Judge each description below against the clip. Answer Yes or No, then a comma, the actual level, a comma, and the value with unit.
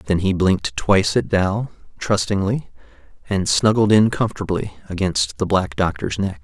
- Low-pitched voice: Yes, very low, 95 Hz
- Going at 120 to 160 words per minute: Yes, average, 150 wpm